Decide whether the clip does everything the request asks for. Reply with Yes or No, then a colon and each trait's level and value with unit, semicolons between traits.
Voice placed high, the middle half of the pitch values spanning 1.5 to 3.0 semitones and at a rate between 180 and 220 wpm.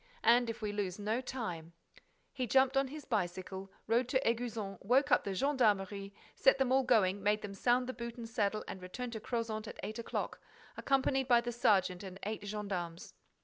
No: high, 220 Hz; average, 4.1 semitones; average, 190 wpm